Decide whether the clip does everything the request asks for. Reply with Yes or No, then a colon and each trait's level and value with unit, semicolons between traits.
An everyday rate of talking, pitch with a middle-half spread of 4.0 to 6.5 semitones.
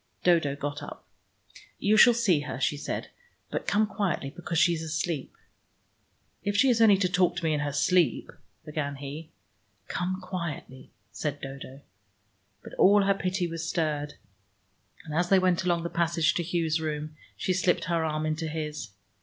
No: average, 175 wpm; average, 3.4 semitones